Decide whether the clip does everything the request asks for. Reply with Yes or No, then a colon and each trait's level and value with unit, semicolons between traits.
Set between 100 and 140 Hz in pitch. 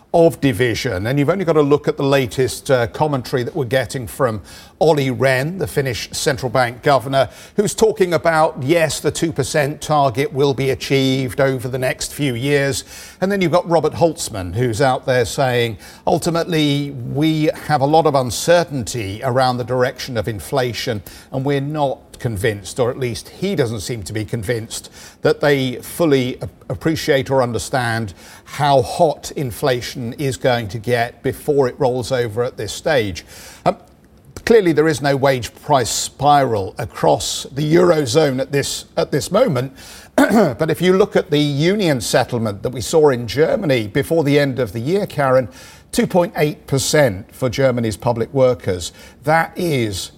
Yes: low, 135 Hz